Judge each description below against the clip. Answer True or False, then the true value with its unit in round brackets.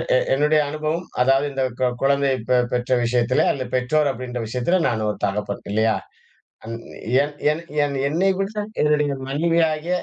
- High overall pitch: False (140 Hz)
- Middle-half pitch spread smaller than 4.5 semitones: True (3.7 semitones)